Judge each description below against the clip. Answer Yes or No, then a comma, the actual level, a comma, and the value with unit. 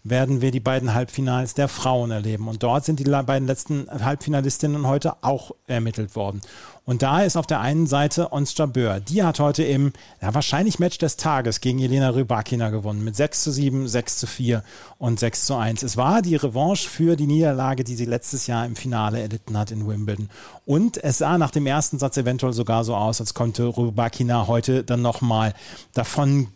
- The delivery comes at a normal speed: No, fast, 200 wpm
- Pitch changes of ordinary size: Yes, average, 3.7 semitones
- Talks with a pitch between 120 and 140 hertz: Yes, low, 130 Hz